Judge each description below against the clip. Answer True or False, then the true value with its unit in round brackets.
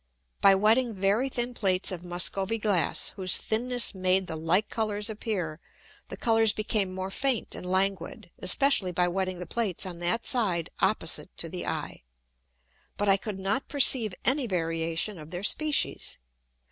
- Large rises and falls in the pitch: False (3.6 semitones)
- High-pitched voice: True (195 Hz)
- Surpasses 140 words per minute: True (160 wpm)